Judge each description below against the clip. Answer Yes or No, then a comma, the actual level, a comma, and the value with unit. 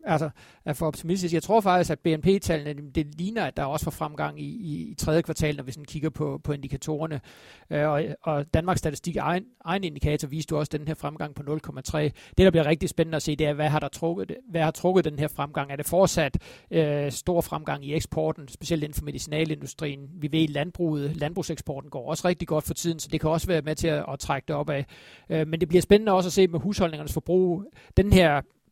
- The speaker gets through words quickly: Yes, fast, 230 wpm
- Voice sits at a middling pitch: Yes, medium, 155 Hz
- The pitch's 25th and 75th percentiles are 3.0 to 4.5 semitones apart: No, narrow, 2.4 semitones